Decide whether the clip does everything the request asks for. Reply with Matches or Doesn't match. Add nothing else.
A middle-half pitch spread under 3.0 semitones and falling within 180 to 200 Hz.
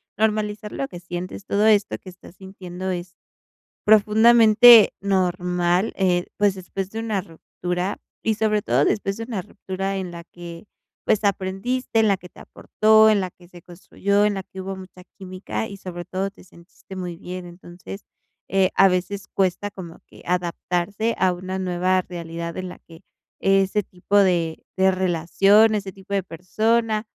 Matches